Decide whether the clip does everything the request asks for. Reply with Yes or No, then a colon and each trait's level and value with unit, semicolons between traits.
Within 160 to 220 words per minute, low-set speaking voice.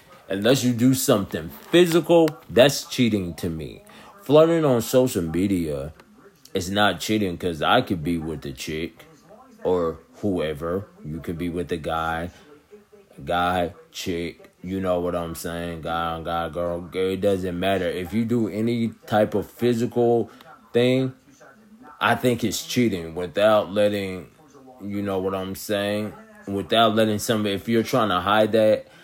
No: average, 150 wpm; low, 105 Hz